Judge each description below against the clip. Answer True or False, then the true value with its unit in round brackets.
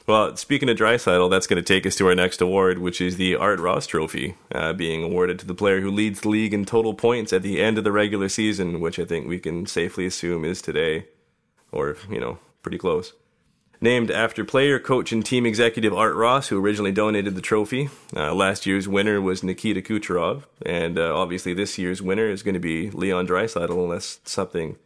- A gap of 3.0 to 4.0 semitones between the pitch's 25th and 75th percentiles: True (3.3 semitones)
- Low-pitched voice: True (100 Hz)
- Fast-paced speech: True (210 wpm)